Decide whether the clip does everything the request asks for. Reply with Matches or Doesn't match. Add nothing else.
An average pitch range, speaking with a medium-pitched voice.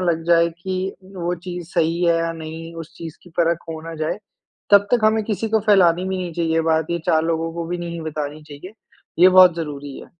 Doesn't match